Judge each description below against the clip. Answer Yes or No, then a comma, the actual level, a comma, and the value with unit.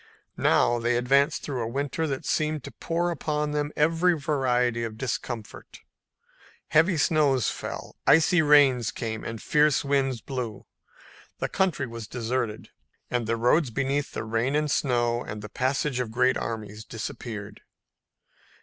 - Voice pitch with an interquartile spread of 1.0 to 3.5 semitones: No, average, 4.2 semitones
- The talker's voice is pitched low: Yes, low, 130 Hz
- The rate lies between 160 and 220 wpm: No, average, 145 wpm